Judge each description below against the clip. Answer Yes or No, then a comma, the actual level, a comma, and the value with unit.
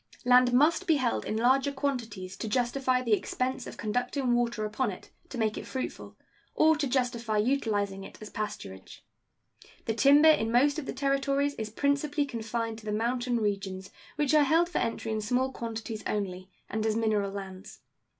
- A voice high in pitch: Yes, high, 240 Hz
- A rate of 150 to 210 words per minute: Yes, average, 180 wpm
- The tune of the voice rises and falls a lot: No, average, 4.2 semitones